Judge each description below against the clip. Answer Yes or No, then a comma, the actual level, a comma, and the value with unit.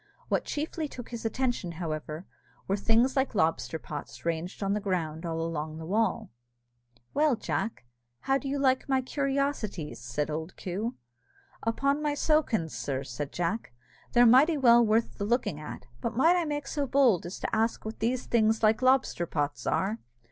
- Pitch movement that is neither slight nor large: No, wide, 8.0 semitones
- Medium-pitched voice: No, high, 220 Hz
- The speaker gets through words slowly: No, average, 170 wpm